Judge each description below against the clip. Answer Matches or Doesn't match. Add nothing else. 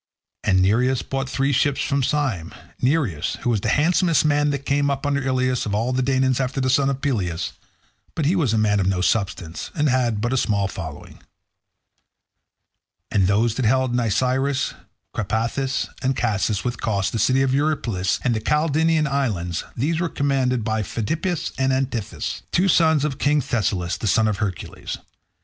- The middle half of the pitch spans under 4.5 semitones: Doesn't match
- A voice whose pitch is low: Matches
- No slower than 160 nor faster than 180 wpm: Matches